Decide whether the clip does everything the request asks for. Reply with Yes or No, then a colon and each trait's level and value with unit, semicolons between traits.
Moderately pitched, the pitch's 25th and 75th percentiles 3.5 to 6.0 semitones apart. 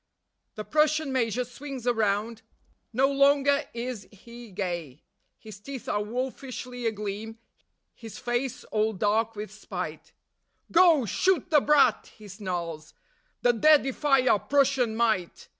No: high, 235 Hz; average, 4.3 semitones